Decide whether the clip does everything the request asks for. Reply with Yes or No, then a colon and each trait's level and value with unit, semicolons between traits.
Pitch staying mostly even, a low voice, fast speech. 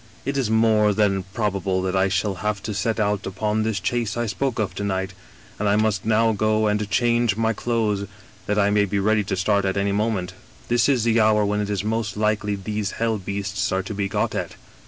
Yes: narrow, 1.8 semitones; low, 105 Hz; fast, 230 wpm